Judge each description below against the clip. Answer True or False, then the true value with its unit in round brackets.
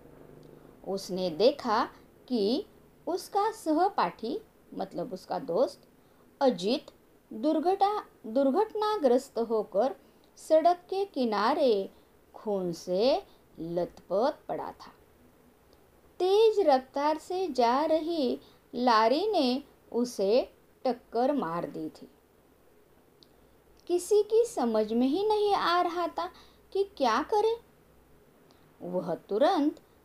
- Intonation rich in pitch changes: True (8.1 semitones)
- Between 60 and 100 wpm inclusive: True (90 wpm)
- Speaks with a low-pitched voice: False (285 Hz)